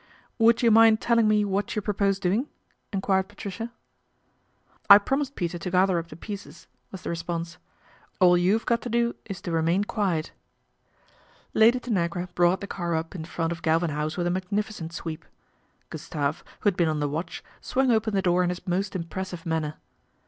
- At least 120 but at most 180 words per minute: No, average, 190 wpm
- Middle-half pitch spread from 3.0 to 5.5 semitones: Yes, average, 3.7 semitones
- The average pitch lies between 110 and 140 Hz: No, medium, 185 Hz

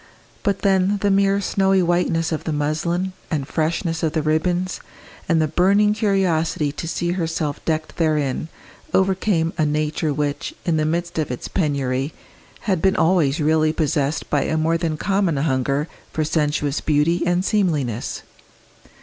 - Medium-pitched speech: Yes, medium, 160 Hz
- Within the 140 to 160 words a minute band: Yes, average, 155 wpm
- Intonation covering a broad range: No, average, 3.3 semitones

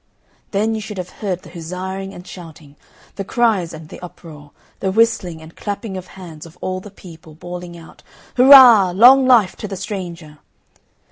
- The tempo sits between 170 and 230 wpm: Yes, average, 175 wpm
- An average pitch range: Yes, average, 3.7 semitones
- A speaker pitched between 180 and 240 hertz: Yes, medium, 185 Hz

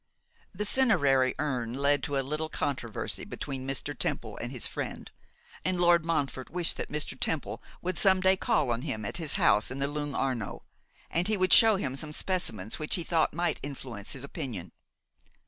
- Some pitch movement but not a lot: Yes, average, 5.0 semitones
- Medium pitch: Yes, medium, 145 Hz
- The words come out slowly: No, average, 185 wpm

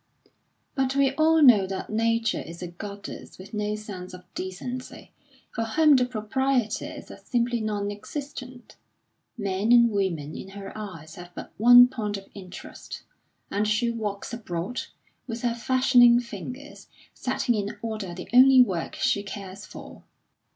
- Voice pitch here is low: No, high, 215 Hz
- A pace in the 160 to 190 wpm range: No, average, 150 wpm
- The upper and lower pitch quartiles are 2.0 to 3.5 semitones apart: No, average, 3.9 semitones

